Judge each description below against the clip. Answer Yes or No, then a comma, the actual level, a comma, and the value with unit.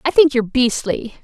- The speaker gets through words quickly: No, average, 195 wpm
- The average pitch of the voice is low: No, very high, 260 Hz